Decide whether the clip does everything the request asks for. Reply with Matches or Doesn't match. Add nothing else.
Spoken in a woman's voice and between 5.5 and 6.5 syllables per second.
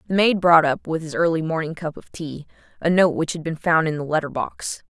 Matches